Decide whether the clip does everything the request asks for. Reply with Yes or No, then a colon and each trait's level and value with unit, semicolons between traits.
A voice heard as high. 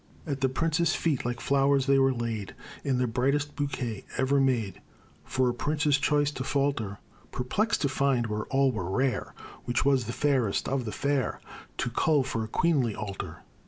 No: low, 130 Hz